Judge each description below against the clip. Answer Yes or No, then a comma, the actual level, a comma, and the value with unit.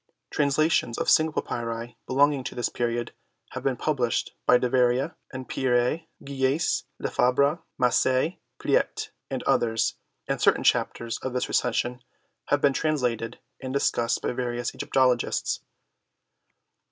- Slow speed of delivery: Yes, slow, 130 wpm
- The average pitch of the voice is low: Yes, low, 125 Hz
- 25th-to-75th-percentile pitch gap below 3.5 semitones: Yes, narrow, 2.5 semitones